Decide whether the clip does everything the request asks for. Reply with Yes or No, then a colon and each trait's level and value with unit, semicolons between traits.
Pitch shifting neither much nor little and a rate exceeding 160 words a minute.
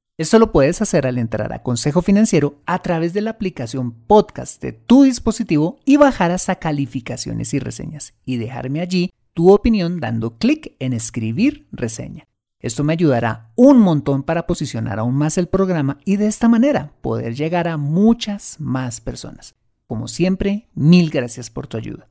No: wide, 7.9 semitones; average, 170 wpm